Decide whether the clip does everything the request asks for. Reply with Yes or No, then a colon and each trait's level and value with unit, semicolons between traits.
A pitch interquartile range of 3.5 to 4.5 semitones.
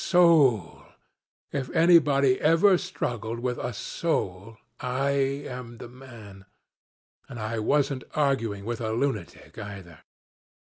Yes: average, 4.2 semitones